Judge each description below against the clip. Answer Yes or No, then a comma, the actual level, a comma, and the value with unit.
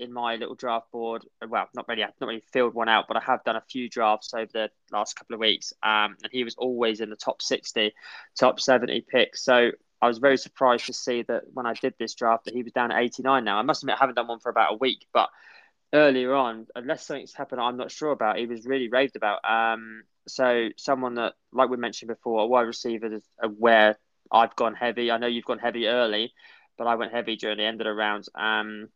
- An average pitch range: No, narrow, 1.9 semitones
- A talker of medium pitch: No, low, 115 Hz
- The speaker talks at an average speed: No, fast, 245 wpm